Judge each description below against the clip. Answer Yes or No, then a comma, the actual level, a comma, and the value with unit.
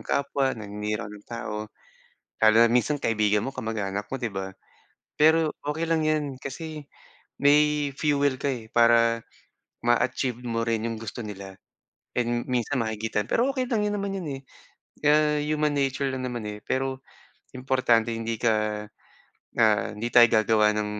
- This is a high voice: No, low, 120 Hz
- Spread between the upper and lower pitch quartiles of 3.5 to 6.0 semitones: Yes, average, 4.7 semitones